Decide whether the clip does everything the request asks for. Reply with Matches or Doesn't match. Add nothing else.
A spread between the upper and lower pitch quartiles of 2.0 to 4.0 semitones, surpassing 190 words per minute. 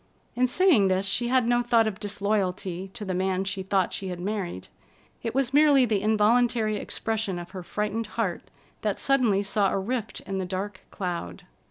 Doesn't match